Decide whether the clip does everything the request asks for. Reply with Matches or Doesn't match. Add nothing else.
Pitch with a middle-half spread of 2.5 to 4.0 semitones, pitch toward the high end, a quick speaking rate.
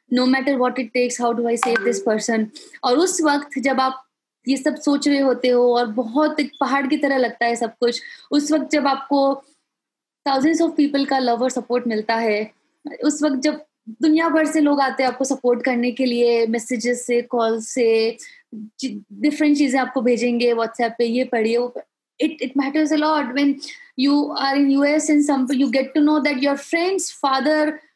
Doesn't match